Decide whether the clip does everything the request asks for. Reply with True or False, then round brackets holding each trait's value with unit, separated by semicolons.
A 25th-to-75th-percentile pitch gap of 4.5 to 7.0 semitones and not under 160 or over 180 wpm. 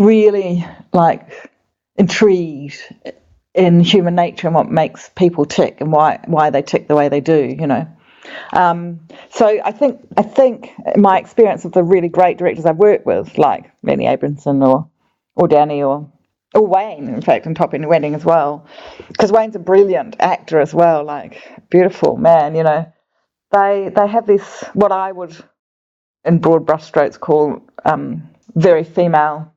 True (4.8 semitones; 165 wpm)